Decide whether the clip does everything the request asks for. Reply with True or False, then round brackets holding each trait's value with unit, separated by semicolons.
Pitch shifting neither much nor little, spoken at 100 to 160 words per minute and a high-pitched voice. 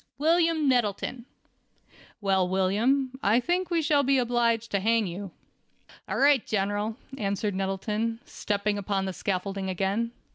True (4.8 semitones; 135 wpm; 215 Hz)